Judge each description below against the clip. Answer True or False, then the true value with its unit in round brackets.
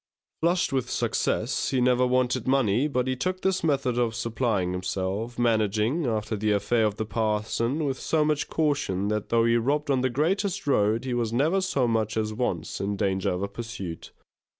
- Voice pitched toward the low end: True (120 Hz)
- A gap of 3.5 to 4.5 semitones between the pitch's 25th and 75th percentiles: True (4.2 semitones)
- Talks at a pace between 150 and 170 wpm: False (195 wpm)